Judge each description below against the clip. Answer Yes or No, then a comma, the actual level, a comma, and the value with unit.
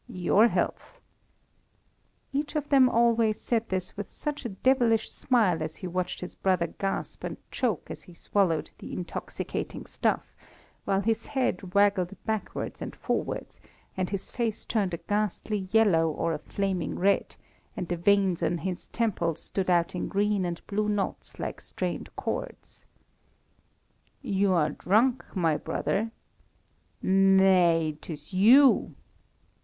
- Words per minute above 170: No, average, 140 wpm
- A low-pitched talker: No, high, 195 Hz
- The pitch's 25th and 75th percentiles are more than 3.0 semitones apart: Yes, average, 3.8 semitones